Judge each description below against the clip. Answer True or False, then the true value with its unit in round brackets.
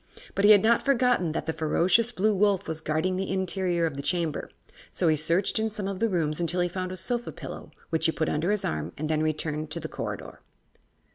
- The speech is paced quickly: True (230 wpm)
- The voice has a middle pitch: True (175 Hz)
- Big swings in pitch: False (4.1 semitones)